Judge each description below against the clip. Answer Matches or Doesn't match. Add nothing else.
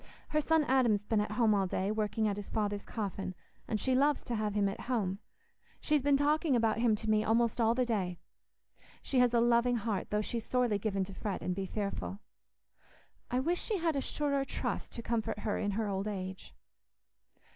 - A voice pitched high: Matches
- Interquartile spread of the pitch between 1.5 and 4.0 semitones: Matches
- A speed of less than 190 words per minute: Doesn't match